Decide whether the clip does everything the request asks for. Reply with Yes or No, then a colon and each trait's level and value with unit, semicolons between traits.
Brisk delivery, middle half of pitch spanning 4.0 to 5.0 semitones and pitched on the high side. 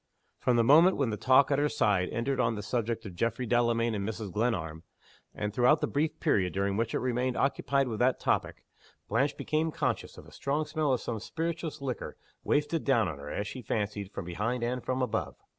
No: fast, 210 wpm; average, 4.7 semitones; low, 120 Hz